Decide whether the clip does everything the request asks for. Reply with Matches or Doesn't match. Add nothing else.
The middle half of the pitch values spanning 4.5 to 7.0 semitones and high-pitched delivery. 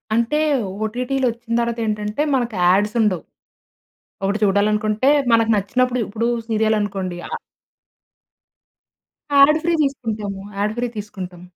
Doesn't match